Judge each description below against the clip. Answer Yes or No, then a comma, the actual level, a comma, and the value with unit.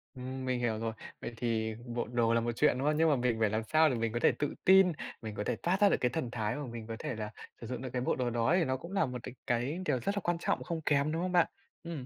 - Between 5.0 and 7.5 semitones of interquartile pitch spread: Yes, average, 5.3 semitones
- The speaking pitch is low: Yes, low, 125 Hz